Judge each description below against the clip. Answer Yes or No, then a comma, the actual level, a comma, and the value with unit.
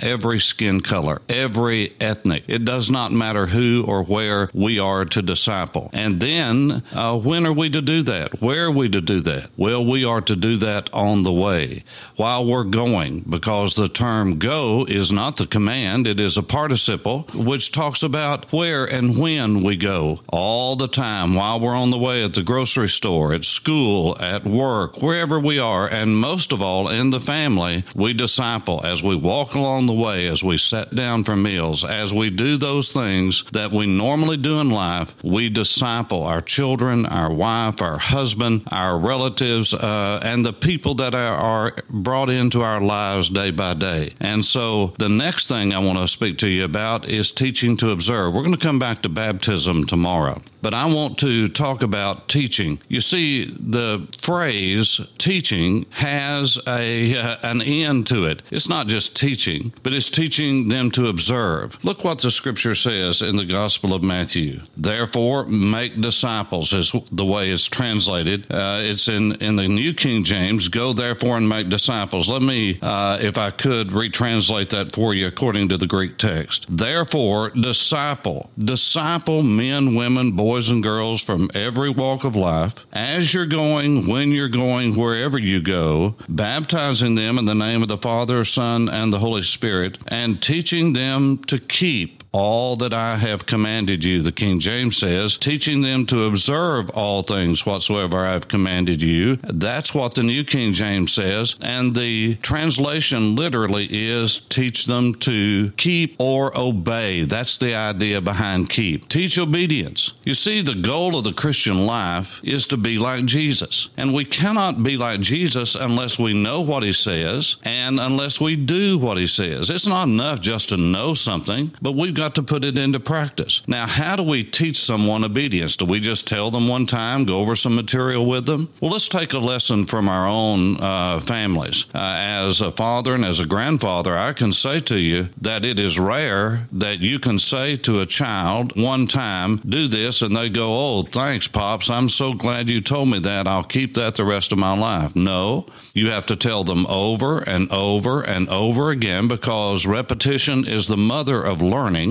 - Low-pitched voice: Yes, low, 115 Hz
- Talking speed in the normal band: Yes, average, 185 wpm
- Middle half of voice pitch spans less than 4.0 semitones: No, average, 4.7 semitones